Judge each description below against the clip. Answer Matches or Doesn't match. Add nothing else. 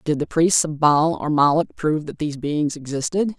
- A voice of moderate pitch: Matches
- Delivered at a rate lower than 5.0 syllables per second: Doesn't match